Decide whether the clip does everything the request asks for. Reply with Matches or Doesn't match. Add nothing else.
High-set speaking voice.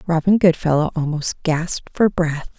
Doesn't match